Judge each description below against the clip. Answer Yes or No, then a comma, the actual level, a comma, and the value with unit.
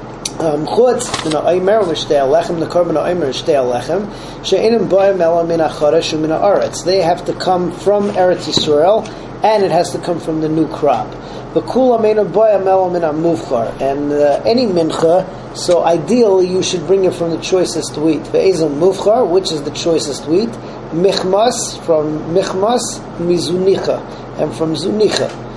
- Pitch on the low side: No, medium, 175 Hz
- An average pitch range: Yes, average, 3.2 semitones